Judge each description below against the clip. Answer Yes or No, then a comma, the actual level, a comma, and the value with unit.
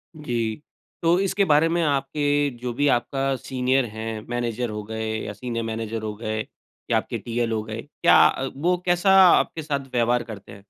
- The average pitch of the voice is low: Yes, low, 120 Hz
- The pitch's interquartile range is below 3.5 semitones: No, average, 4.5 semitones